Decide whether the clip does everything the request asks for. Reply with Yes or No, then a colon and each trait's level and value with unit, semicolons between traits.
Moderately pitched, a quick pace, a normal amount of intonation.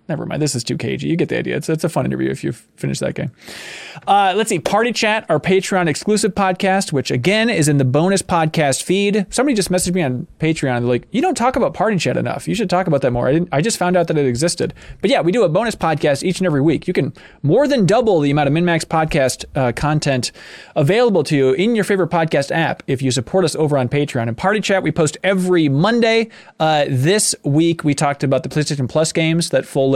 Yes: medium, 160 Hz; fast, 250 wpm; average, 5.0 semitones